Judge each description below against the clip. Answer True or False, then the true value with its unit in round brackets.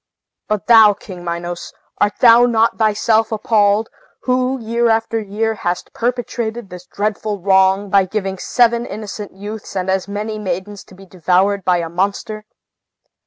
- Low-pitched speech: False (210 Hz)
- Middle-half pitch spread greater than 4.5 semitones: False (2.8 semitones)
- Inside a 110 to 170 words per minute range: True (150 wpm)